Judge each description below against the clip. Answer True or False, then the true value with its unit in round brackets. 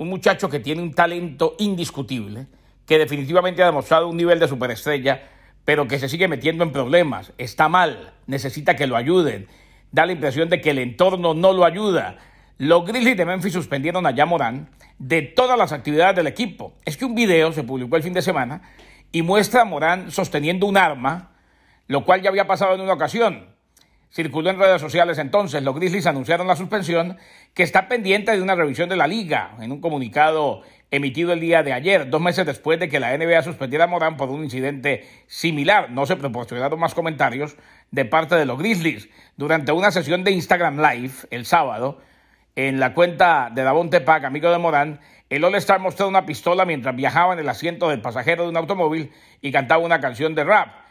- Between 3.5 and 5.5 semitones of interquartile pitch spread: True (4.3 semitones)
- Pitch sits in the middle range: True (165 Hz)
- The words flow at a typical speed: False (195 wpm)